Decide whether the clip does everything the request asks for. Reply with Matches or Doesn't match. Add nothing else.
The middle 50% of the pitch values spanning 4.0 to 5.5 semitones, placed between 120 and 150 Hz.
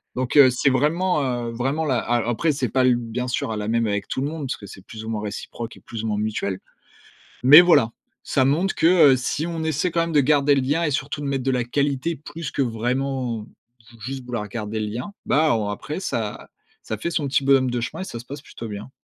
Matches